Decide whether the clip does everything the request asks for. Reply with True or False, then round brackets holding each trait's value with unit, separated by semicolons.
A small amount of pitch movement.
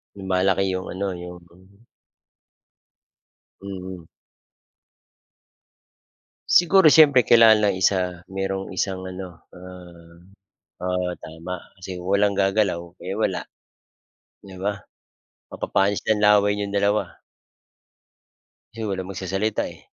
True (1.9 semitones)